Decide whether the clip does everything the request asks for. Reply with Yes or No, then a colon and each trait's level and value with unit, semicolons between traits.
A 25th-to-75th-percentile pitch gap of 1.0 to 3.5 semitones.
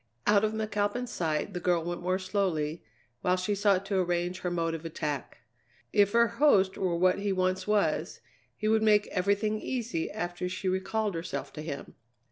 Yes: average, 3.1 semitones